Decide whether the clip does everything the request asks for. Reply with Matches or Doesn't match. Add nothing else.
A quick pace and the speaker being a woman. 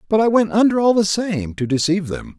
Doesn't match